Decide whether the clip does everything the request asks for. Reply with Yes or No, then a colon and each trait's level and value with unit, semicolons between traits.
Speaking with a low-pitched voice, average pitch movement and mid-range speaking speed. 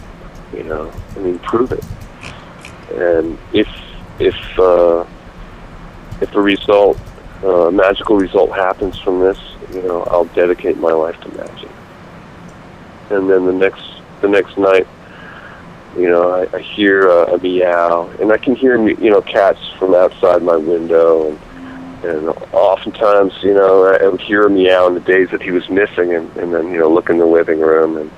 No: very low, 90 Hz; narrow, 2.0 semitones; average, 175 wpm